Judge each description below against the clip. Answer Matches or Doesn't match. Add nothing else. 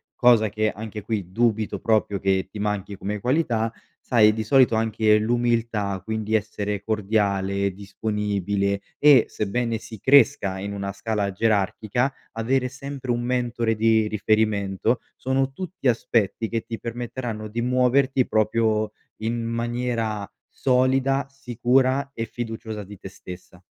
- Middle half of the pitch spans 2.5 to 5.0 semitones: Matches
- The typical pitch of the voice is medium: Doesn't match